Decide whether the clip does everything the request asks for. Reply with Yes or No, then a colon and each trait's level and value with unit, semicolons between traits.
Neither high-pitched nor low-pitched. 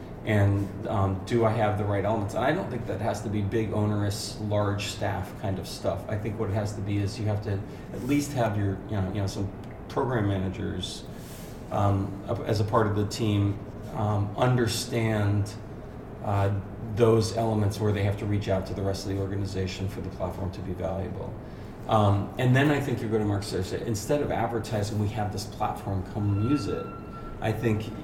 No: low, 105 Hz